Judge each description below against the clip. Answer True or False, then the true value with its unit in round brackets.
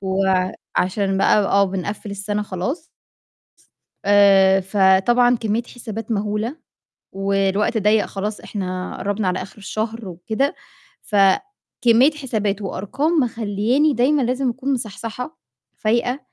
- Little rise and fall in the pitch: False (3.6 semitones)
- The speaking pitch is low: False (210 Hz)